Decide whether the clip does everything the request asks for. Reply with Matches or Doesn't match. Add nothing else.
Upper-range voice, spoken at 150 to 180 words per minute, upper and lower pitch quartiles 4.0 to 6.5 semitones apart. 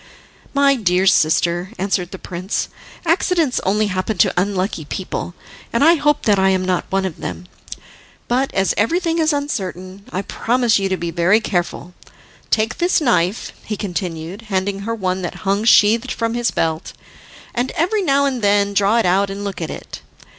Matches